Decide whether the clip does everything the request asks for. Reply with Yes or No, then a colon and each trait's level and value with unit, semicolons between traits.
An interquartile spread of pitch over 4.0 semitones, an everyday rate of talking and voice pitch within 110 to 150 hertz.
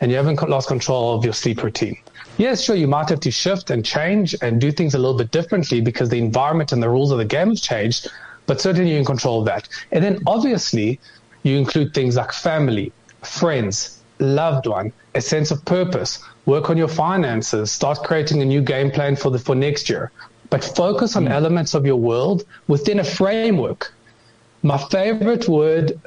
Yes: average, 5.2 semitones; average, 195 wpm; medium, 140 Hz